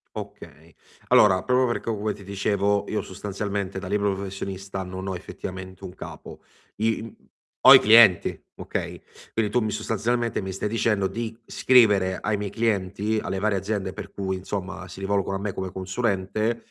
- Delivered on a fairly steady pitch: Yes, narrow, 2.3 semitones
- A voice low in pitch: Yes, low, 100 Hz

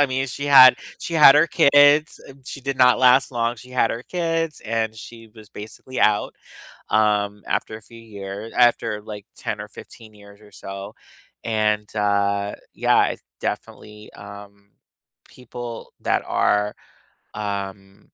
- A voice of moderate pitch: No, low, 110 Hz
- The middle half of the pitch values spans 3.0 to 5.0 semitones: Yes, average, 3.7 semitones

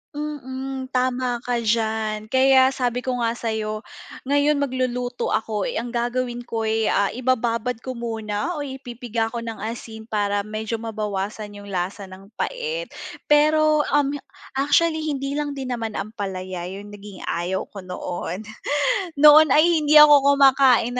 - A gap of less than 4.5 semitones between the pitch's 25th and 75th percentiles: Yes, average, 4.1 semitones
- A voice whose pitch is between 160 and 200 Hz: No, high, 240 Hz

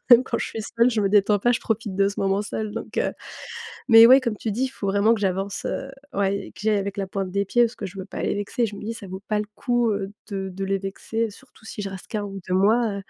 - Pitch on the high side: Yes, high, 205 Hz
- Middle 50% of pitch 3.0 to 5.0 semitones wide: No, narrow, 2.5 semitones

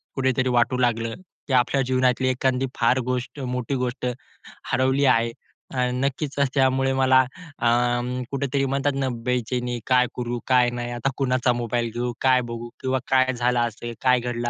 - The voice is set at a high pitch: No, low, 125 Hz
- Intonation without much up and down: Yes, narrow, 1.4 semitones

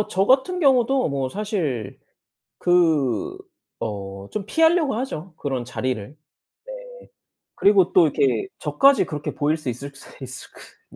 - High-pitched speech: No, medium, 155 Hz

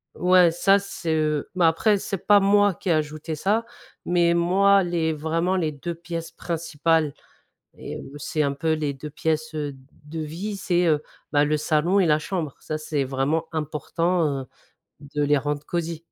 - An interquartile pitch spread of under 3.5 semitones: Yes, average, 2.8 semitones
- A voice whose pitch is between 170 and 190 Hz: No, medium, 160 Hz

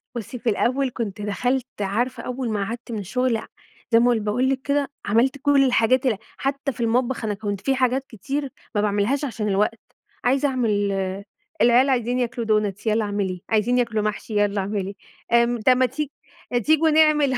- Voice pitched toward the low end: No, high, 240 Hz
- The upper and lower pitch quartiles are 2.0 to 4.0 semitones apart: Yes, average, 3.7 semitones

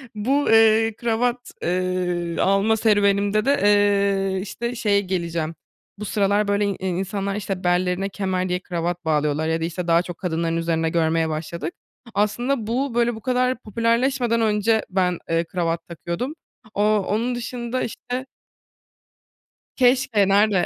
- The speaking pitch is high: Yes, high, 200 Hz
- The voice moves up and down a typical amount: Yes, average, 4.2 semitones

